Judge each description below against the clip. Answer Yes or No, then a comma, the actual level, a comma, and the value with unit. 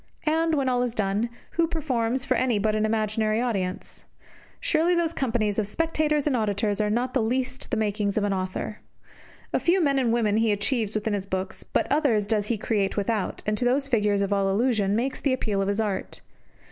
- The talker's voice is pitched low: No, high, 220 Hz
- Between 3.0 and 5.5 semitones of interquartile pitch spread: Yes, average, 4.1 semitones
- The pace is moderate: No, fast, 215 wpm